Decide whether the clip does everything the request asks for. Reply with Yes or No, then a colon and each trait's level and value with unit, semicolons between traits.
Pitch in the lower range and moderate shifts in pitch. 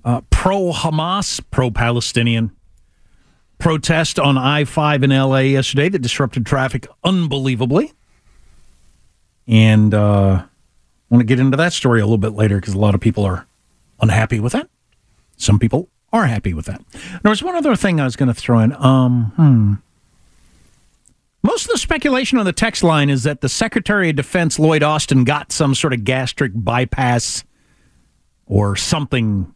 No: low, 130 Hz; wide, 6.0 semitones